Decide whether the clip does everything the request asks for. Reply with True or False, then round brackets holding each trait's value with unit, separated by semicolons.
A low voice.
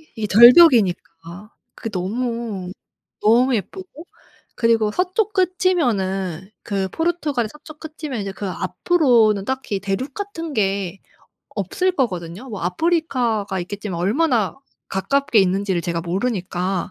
False (220 Hz)